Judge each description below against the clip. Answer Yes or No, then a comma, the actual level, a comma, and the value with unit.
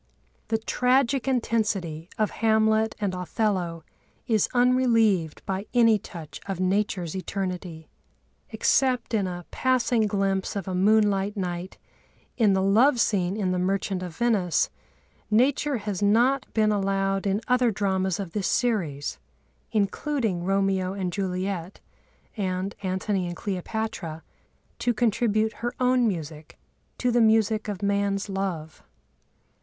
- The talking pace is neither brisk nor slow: No, slow, 130 wpm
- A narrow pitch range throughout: No, average, 3.2 semitones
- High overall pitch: Yes, high, 200 Hz